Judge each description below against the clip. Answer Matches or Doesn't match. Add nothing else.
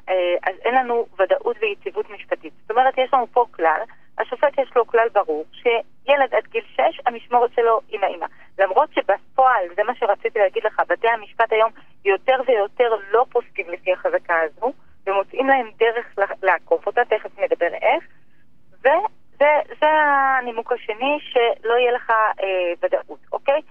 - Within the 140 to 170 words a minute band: Matches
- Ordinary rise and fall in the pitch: Matches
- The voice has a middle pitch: Doesn't match